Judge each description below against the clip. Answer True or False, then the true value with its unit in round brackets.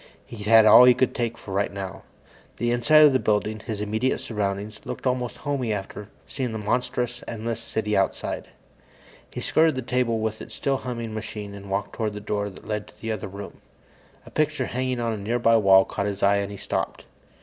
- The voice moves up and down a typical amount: True (3.1 semitones)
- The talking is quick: True (215 wpm)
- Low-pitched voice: True (110 Hz)